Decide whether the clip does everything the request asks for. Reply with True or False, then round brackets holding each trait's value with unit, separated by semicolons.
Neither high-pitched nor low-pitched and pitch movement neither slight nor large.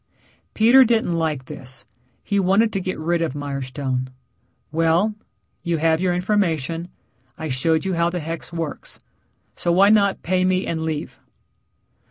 True (170 Hz; 3.2 semitones)